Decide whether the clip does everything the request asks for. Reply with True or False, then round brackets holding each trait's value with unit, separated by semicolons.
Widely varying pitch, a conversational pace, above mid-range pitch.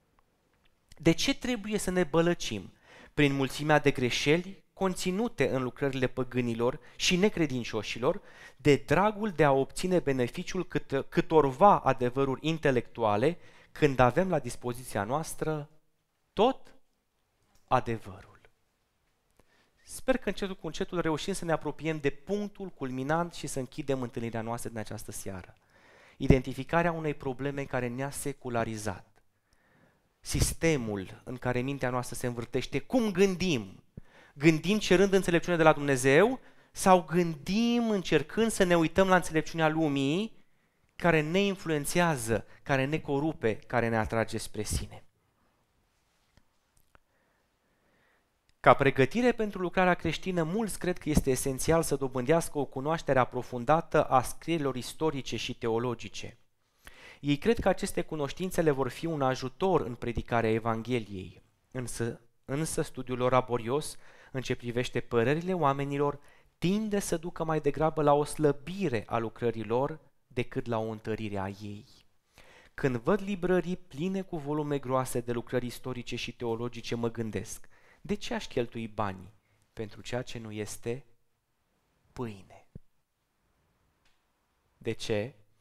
False (5.8 semitones; 125 wpm; 140 Hz)